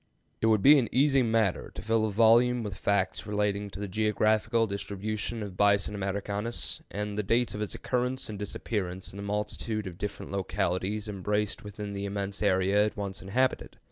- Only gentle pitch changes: Yes, narrow, 1.8 semitones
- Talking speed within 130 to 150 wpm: No, average, 180 wpm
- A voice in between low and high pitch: No, low, 105 Hz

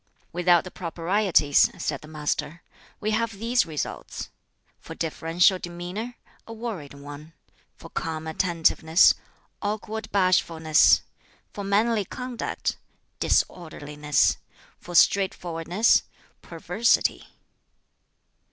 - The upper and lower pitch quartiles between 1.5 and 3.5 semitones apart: No, average, 4.5 semitones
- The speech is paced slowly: Yes, slow, 90 wpm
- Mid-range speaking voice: Yes, medium, 175 Hz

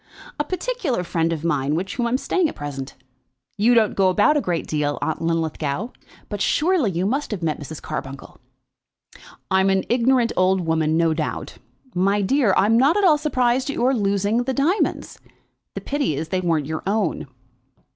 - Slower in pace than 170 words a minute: No, average, 185 wpm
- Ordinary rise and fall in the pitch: No, wide, 7.7 semitones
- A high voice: Yes, high, 195 Hz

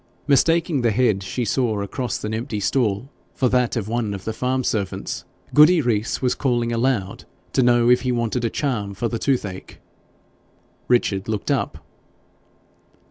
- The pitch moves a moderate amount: Yes, average, 3.2 semitones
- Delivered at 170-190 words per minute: No, average, 160 wpm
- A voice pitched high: No, low, 120 Hz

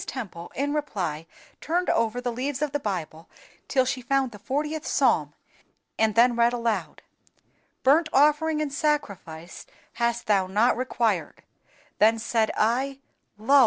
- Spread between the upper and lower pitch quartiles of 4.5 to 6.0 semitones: Yes, average, 4.8 semitones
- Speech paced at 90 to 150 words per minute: Yes, average, 140 wpm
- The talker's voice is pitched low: No, high, 240 Hz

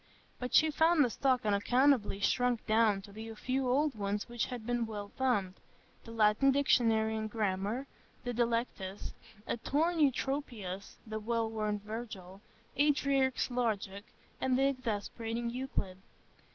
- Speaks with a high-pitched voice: Yes, high, 230 Hz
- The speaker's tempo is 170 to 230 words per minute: No, slow, 135 wpm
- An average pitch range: Yes, average, 3.7 semitones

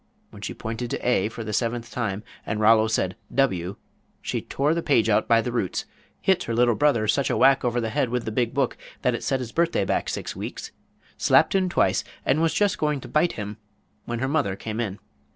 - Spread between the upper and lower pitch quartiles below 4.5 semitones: Yes, average, 4.0 semitones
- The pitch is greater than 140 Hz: No, low, 120 Hz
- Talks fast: Yes, fast, 225 wpm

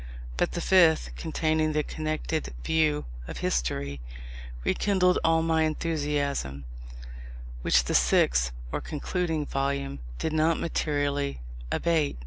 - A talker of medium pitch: Yes, medium, 155 Hz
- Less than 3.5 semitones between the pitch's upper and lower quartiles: Yes, average, 2.7 semitones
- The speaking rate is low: Yes, slow, 115 wpm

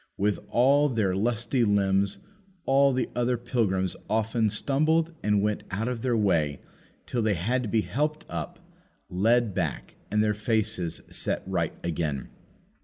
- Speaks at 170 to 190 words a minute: No, average, 150 wpm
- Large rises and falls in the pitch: No, average, 4.1 semitones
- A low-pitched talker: Yes, low, 110 Hz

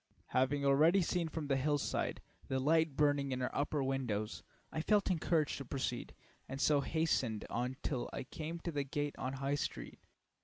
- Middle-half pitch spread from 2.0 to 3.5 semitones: Yes, average, 2.9 semitones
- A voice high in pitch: No, medium, 140 Hz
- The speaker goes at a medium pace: Yes, average, 180 wpm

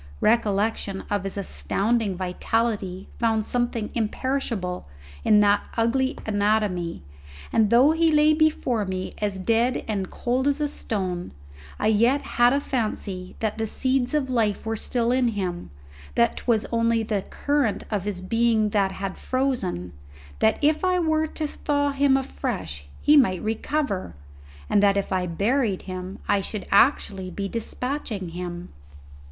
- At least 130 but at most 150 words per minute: Yes, average, 145 wpm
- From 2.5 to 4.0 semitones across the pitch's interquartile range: No, average, 4.9 semitones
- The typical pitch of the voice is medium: No, high, 220 Hz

